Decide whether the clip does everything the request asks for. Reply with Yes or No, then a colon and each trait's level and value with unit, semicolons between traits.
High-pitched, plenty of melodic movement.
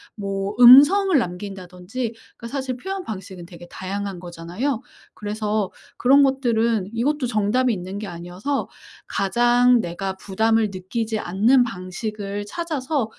No: high, 215 Hz; average, 4.7 semitones